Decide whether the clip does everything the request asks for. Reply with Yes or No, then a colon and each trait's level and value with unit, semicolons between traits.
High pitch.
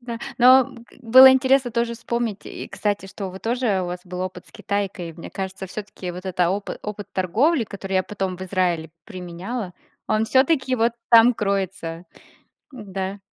Yes: high, 200 Hz